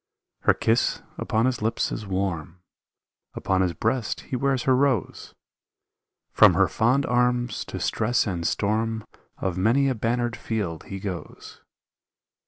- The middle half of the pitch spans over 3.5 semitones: Yes, average, 4.2 semitones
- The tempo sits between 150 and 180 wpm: No, average, 140 wpm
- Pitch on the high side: No, low, 115 Hz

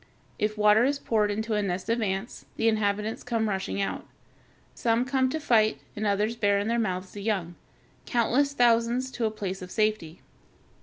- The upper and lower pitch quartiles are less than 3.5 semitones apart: Yes, narrow, 2.4 semitones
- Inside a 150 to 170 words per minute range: No, average, 195 wpm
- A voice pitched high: Yes, high, 215 Hz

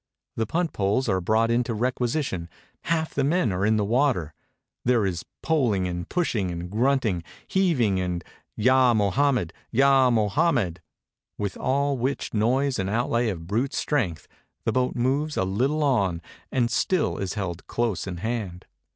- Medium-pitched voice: No, low, 115 Hz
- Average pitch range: No, wide, 5.8 semitones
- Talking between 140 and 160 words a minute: Yes, average, 155 wpm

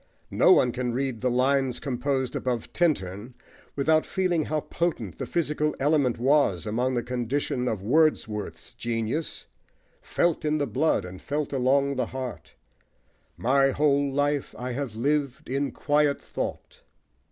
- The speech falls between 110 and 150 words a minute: Yes, average, 140 wpm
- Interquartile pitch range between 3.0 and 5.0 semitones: Yes, average, 3.3 semitones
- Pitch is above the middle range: No, low, 135 Hz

